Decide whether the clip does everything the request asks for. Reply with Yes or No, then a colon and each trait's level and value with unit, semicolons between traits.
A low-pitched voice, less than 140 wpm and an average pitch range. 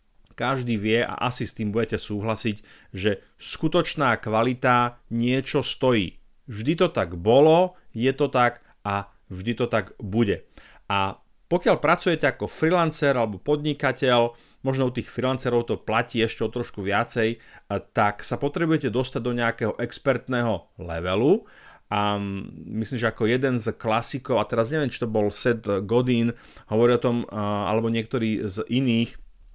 No: low, 120 Hz; average, 145 wpm; average, 3.1 semitones